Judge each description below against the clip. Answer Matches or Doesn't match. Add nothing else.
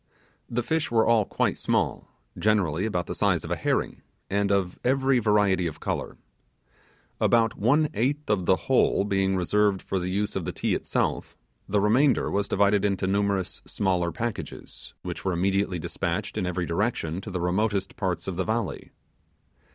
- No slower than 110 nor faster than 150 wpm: Doesn't match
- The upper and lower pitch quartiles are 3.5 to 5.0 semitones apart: Doesn't match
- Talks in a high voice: Doesn't match